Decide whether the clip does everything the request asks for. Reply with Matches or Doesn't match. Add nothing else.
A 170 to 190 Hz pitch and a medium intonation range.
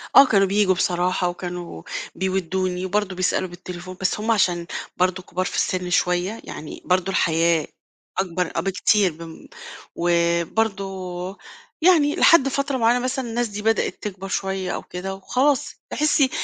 Matches